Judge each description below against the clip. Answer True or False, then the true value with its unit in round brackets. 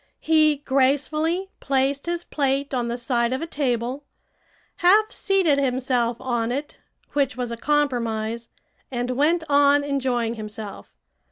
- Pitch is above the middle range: True (270 Hz)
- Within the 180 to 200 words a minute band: False (135 wpm)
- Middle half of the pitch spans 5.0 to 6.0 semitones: False (3.5 semitones)